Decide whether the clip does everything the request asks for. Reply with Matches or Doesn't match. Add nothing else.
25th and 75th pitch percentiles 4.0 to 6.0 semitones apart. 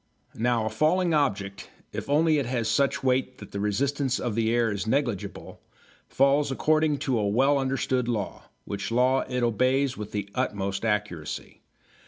Matches